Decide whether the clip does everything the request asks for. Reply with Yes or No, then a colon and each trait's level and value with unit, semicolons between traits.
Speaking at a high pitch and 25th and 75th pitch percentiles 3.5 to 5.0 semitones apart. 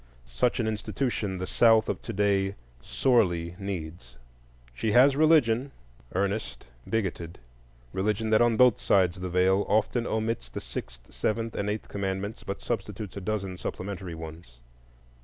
No: low, 100 Hz; average, 3.8 semitones